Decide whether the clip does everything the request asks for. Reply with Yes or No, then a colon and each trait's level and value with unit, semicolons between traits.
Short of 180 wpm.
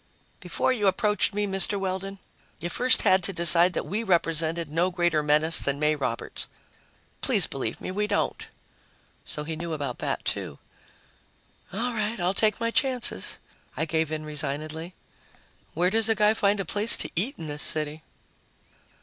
Yes: average, 165 wpm